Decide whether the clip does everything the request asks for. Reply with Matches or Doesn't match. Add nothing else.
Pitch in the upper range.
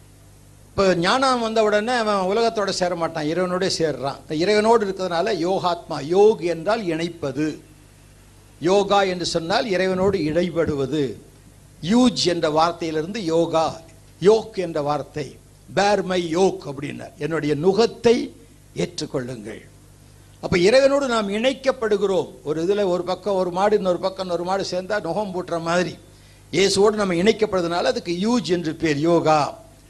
Doesn't match